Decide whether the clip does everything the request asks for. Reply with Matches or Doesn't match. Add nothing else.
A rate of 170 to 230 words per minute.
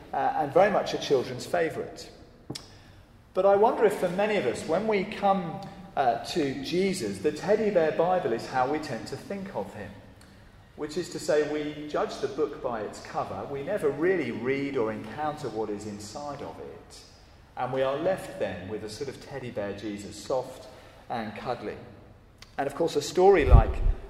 Matches